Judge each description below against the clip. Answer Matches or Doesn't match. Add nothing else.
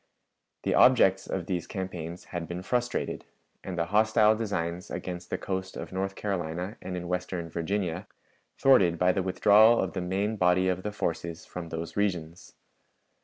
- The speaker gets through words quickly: Doesn't match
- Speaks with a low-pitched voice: Matches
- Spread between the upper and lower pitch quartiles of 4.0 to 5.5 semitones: Doesn't match